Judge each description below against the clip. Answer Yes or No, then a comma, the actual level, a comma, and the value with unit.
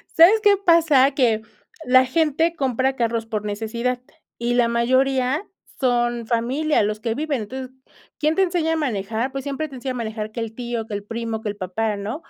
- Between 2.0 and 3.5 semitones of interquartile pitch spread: No, average, 4.0 semitones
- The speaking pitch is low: No, high, 245 Hz